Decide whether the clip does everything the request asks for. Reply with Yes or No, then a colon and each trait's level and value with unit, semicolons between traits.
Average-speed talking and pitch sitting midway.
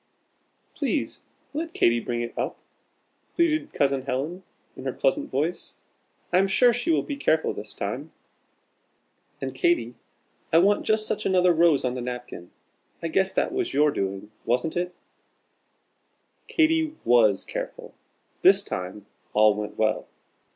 Yes: average, 145 wpm; medium, 165 Hz